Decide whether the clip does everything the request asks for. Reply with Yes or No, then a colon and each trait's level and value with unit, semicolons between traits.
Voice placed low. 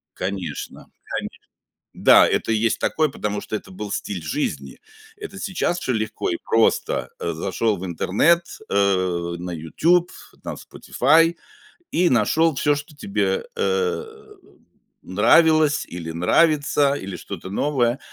Yes: low, 120 Hz